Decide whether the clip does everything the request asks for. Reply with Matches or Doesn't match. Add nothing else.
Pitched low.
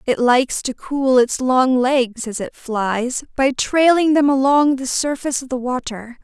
Doesn't match